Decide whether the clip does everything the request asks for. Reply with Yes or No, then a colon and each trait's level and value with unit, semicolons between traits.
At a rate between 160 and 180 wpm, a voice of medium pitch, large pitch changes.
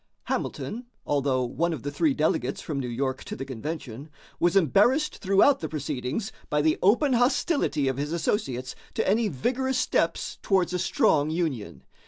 Yes: average, 165 wpm; medium, 155 Hz; wide, 7.0 semitones